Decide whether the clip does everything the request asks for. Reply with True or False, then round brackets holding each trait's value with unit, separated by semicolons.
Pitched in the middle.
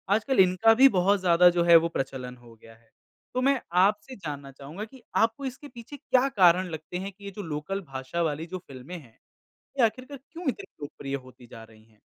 True (180 Hz)